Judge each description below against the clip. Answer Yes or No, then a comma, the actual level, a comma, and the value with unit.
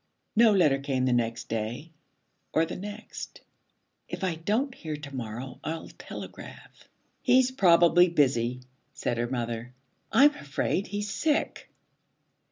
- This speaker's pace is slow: Yes, slow, 130 wpm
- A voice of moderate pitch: Yes, medium, 155 Hz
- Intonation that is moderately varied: No, wide, 8.2 semitones